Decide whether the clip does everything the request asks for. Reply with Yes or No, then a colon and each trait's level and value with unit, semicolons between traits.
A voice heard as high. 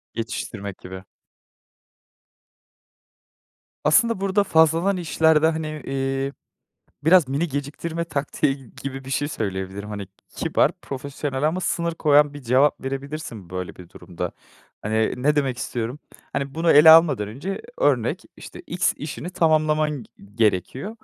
No: medium, 145 Hz